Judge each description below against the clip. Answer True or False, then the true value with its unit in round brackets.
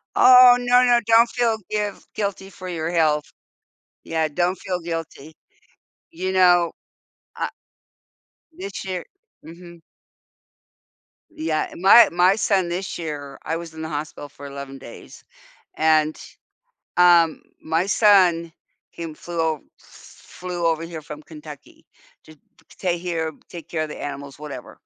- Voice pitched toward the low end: False (170 Hz)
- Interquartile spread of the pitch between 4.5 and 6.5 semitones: False (3.0 semitones)